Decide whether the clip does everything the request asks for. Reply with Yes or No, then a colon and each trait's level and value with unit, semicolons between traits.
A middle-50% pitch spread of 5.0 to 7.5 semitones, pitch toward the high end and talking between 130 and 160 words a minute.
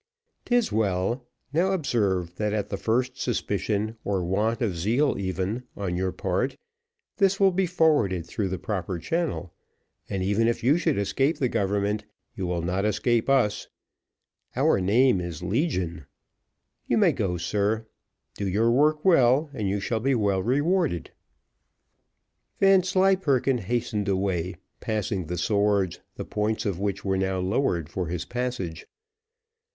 No: wide, 5.4 semitones; low, 105 Hz; average, 145 wpm